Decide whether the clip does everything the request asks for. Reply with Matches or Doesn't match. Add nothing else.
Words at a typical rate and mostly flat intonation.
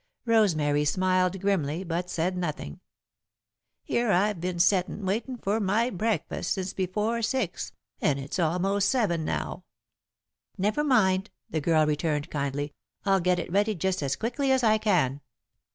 Doesn't match